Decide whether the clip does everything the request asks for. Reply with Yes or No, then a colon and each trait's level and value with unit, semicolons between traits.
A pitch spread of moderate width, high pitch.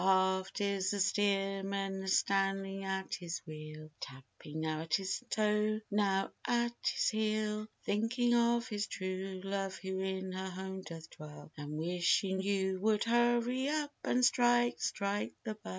No: narrow, 2.3 semitones; high, 195 Hz